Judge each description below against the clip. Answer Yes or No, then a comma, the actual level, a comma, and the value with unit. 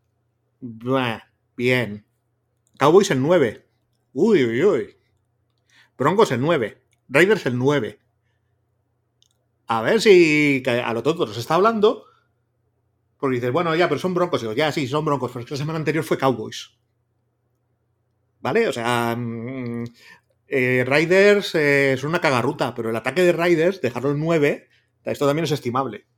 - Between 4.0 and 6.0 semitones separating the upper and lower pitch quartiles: Yes, average, 4.3 semitones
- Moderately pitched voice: No, low, 125 Hz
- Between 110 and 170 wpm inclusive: Yes, average, 145 wpm